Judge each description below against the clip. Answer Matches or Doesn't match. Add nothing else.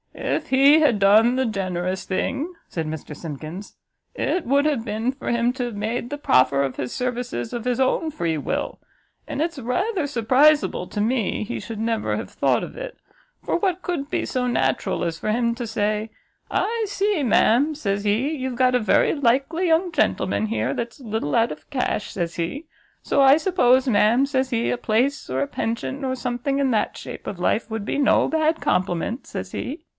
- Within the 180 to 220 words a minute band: Matches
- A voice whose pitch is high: Matches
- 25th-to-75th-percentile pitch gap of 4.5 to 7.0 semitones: Matches